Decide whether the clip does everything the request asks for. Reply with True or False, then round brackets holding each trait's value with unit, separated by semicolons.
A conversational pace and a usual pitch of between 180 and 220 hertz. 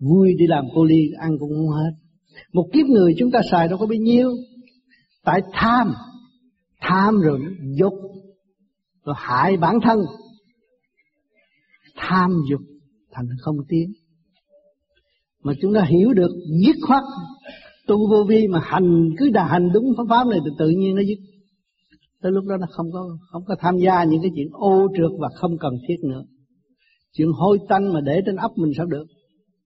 True (180 wpm; 185 Hz)